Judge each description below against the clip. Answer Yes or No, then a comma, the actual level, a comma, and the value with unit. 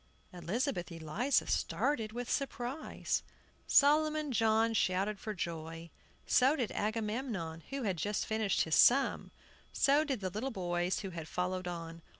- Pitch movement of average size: No, wide, 6.7 semitones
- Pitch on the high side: Yes, high, 215 Hz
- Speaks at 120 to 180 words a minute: Yes, average, 140 wpm